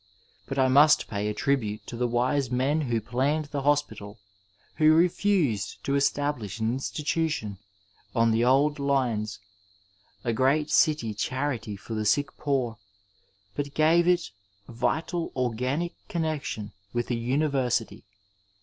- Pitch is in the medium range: No, low, 130 Hz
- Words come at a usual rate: No, slow, 130 wpm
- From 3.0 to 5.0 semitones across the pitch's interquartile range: Yes, average, 4.4 semitones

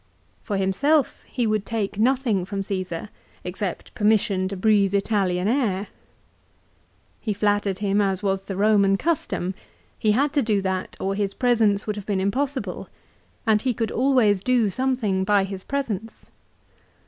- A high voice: Yes, high, 205 Hz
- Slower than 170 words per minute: Yes, average, 150 wpm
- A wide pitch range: No, average, 2.9 semitones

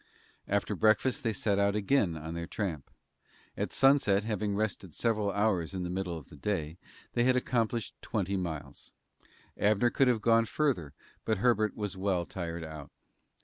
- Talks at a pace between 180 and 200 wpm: No, average, 165 wpm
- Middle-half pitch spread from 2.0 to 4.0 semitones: No, average, 4.4 semitones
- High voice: No, low, 100 Hz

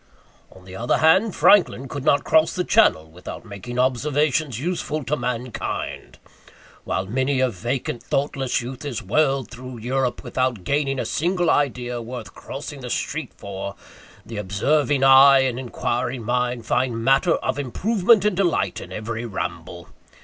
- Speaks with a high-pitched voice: No, low, 130 Hz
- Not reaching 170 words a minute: Yes, average, 150 wpm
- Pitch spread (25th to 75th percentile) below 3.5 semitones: No, average, 3.8 semitones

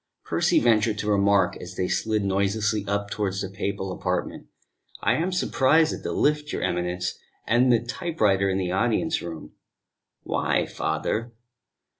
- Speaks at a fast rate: No, average, 160 wpm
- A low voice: Yes, low, 105 Hz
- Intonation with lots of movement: No, average, 3.8 semitones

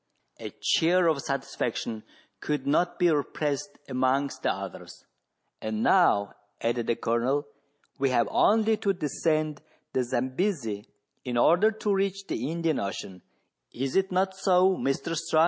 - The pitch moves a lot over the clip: Yes, wide, 6.3 semitones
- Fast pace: No, average, 145 wpm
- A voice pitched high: No, medium, 150 Hz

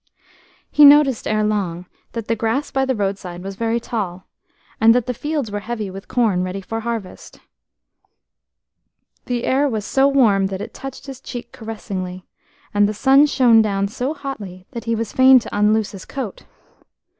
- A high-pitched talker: Yes, high, 225 Hz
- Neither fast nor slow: Yes, average, 175 wpm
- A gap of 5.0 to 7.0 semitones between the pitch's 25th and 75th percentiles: No, average, 4.6 semitones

